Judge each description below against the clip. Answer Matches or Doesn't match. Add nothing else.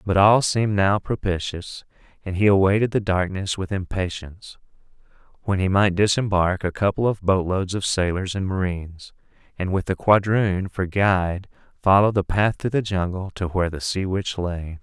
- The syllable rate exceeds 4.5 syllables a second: Matches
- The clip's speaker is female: Doesn't match